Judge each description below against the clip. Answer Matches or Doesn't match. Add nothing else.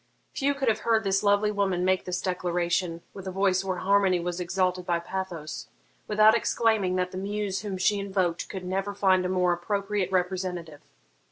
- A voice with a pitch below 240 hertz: Matches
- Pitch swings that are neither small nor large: Doesn't match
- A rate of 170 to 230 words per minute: Matches